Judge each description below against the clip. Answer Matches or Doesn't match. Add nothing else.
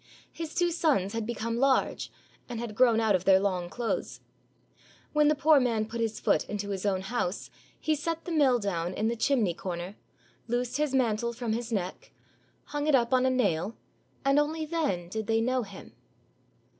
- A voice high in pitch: Matches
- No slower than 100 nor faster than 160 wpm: Doesn't match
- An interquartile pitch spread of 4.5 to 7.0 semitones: Matches